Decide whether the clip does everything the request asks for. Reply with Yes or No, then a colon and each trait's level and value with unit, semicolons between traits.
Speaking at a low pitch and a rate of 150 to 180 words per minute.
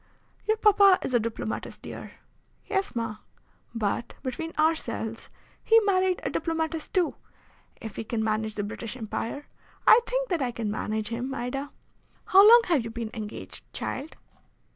No: very high, 260 Hz; average, 155 wpm